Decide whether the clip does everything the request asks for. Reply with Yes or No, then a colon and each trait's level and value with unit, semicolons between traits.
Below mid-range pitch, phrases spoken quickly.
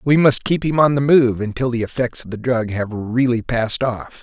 Yes: low, 125 Hz; fast, 240 wpm